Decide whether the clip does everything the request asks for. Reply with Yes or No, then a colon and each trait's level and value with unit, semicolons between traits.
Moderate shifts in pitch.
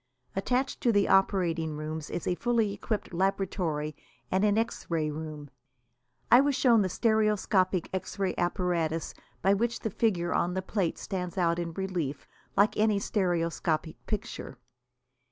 Yes: average, 3.9 semitones